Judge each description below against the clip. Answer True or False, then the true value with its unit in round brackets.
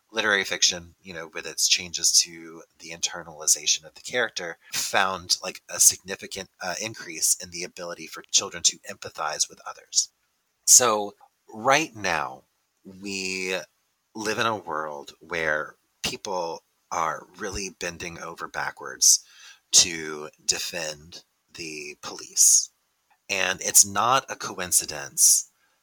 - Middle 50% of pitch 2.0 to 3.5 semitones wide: True (2.8 semitones)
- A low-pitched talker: True (85 Hz)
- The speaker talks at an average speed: False (120 wpm)